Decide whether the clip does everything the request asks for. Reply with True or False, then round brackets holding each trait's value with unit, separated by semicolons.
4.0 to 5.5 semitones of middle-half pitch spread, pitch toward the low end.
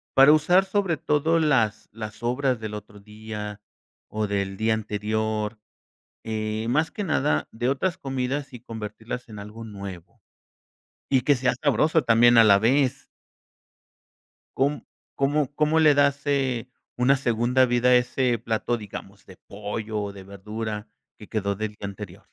True (4.5 semitones; 115 Hz)